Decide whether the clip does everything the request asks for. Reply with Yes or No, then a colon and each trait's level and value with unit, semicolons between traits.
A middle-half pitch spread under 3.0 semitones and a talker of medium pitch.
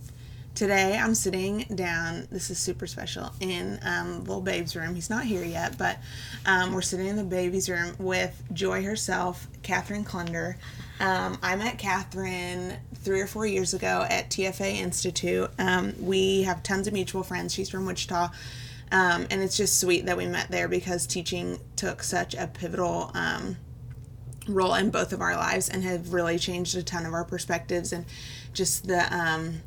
Yes: narrow, 2.6 semitones; medium, 180 Hz